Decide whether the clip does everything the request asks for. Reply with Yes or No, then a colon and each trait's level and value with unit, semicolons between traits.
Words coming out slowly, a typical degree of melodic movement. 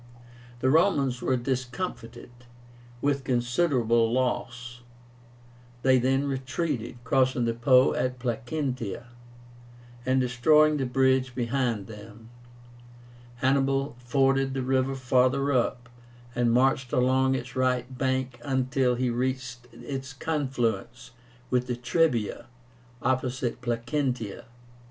No: slow, 105 wpm; narrow, 1.7 semitones